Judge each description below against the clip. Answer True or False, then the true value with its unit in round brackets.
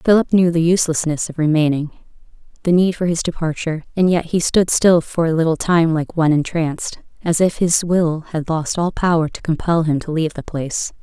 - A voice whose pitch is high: False (165 Hz)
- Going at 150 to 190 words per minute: False (205 wpm)